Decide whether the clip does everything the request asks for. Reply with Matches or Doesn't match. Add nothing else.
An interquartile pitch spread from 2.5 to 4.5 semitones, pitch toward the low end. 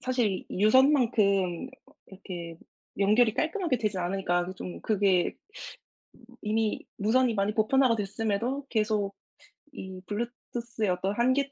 Doesn't match